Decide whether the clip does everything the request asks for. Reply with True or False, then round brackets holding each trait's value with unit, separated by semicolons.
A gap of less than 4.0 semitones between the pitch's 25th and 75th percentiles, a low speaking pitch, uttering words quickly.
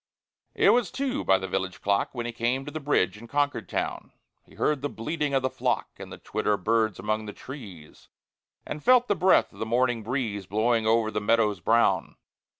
False (5.1 semitones; 115 Hz; 210 wpm)